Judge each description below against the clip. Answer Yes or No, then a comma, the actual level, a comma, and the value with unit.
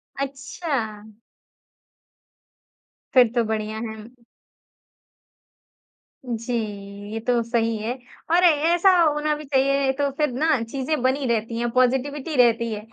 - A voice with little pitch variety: No, average, 3.8 semitones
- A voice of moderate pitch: No, very high, 255 Hz